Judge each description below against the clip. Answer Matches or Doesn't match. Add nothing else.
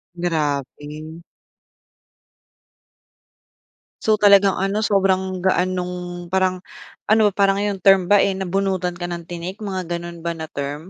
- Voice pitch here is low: Doesn't match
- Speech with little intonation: Matches